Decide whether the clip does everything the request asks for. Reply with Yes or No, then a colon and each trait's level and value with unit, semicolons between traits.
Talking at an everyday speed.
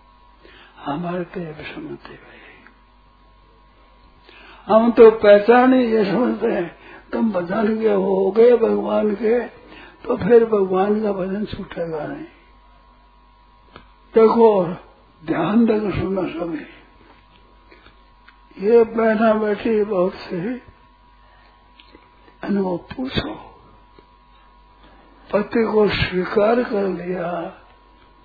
No: slow, 85 wpm